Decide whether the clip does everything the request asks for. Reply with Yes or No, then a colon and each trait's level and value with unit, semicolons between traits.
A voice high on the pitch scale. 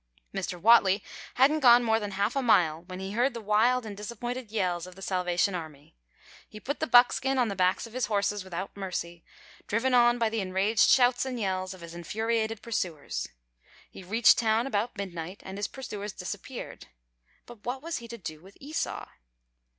Yes: high, 210 Hz